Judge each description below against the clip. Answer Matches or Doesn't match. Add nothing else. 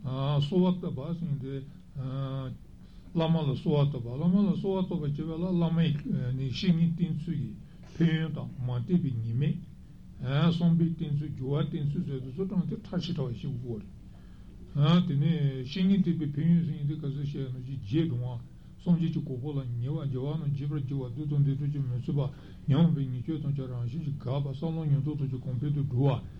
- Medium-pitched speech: Matches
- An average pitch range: Matches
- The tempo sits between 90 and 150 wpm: Doesn't match